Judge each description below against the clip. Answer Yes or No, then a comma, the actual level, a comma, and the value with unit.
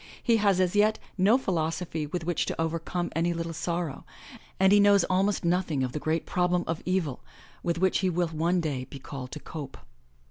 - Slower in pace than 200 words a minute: No, fast, 205 wpm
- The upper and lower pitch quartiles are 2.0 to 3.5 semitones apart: Yes, average, 2.8 semitones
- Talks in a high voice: No, medium, 170 Hz